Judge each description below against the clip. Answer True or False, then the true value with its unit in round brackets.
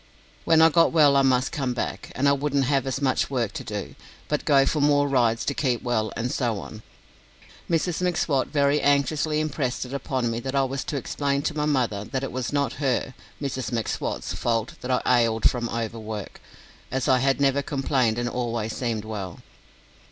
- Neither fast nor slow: True (195 wpm)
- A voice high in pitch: False (130 Hz)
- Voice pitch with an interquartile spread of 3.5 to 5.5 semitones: False (3.1 semitones)